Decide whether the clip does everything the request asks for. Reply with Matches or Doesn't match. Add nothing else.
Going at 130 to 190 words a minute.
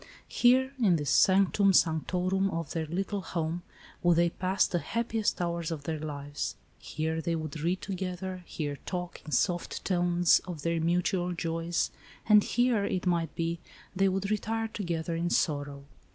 Matches